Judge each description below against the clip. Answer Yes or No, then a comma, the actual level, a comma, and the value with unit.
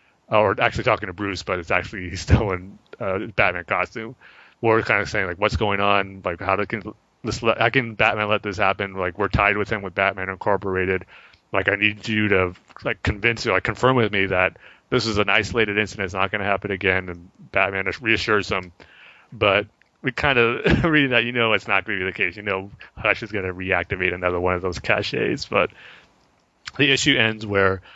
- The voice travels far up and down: No, average, 2.8 semitones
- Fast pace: Yes, fast, 215 wpm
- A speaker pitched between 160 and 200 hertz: No, low, 100 Hz